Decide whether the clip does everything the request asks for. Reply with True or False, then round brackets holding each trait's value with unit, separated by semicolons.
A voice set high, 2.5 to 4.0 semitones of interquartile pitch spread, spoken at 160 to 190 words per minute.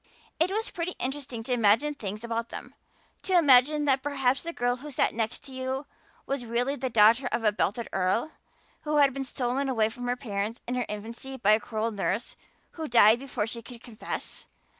False (245 Hz; 3.4 semitones; 200 wpm)